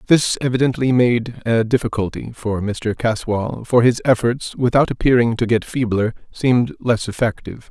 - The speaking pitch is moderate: No, low, 120 Hz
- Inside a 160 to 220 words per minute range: No, average, 150 wpm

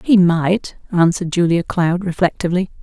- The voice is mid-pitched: Yes, medium, 175 Hz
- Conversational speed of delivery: No, slow, 125 wpm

